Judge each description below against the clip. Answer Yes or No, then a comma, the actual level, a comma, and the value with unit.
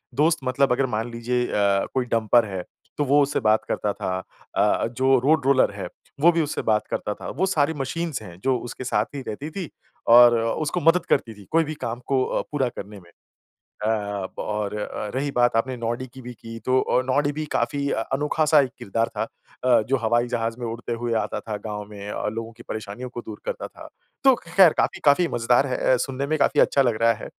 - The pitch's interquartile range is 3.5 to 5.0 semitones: Yes, average, 4.0 semitones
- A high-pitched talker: No, low, 125 Hz